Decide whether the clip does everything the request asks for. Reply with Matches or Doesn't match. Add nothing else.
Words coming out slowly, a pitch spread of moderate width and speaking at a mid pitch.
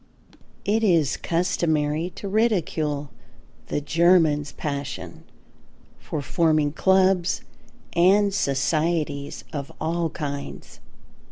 Matches